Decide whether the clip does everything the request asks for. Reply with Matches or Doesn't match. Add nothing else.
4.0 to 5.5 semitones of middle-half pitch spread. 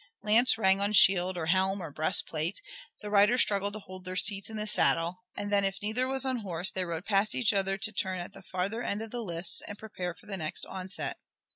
Doesn't match